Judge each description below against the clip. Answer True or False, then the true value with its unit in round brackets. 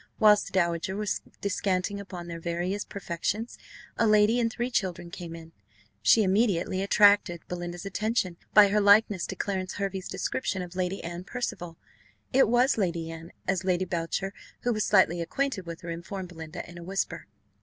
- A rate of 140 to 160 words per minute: False (170 wpm)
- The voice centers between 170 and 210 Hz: True (185 Hz)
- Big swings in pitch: False (3.2 semitones)